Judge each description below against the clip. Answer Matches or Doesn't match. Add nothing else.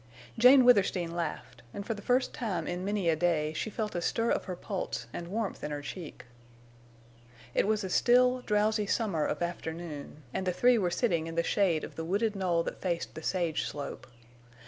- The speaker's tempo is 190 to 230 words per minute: Matches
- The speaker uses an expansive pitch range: Doesn't match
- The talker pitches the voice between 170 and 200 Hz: Matches